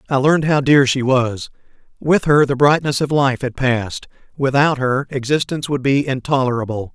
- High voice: No, low, 135 Hz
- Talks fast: No, average, 175 wpm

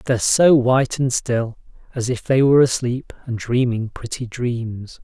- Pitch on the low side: Yes, low, 125 Hz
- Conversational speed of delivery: Yes, average, 165 wpm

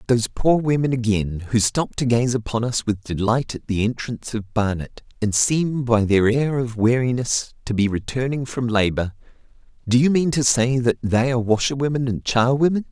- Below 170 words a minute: No, average, 185 wpm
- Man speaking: Yes, male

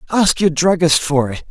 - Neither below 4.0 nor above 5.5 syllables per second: Yes, 4.8 syllables/s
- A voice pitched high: No, medium, 165 Hz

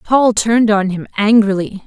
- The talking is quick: No, average, 160 wpm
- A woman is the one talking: Yes, female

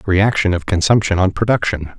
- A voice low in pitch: Yes, very low, 95 Hz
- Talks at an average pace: Yes, average, 150 wpm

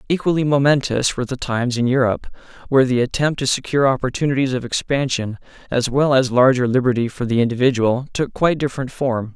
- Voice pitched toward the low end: Yes, low, 130 Hz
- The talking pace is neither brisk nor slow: Yes, average, 175 wpm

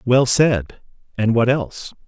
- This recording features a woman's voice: No, male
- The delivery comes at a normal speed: Yes, average, 145 wpm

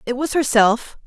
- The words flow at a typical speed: Yes, average, 170 wpm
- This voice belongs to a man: No, female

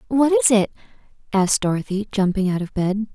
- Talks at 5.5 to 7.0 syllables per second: Yes, 5.8 syllables/s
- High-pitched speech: Yes, high, 205 Hz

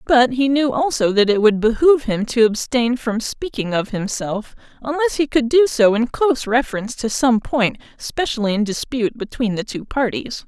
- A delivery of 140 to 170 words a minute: No, average, 190 wpm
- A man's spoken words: No, female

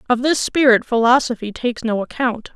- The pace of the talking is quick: No, average, 165 wpm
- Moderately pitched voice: No, high, 240 Hz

